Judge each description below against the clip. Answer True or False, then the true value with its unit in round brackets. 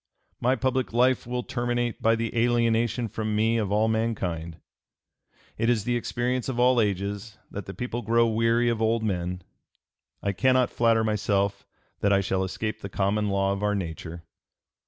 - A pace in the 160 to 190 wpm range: True (170 wpm)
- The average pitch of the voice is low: True (110 Hz)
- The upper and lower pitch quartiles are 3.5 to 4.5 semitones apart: False (3.1 semitones)